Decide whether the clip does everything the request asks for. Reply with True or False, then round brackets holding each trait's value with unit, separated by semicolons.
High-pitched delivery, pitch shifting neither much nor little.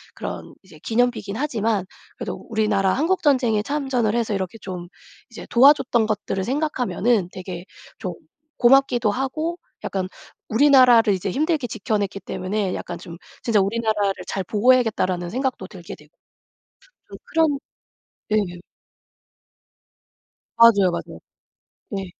True (220 Hz; 4.7 semitones)